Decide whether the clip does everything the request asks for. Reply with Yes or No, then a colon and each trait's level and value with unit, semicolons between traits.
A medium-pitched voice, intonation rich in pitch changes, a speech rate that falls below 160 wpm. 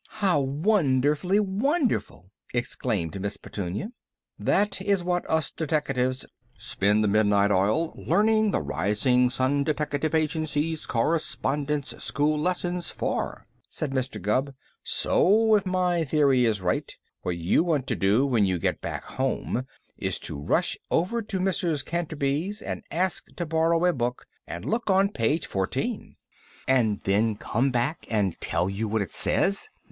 Yes: medium, 145 Hz; wide, 7.9 semitones; average, 145 wpm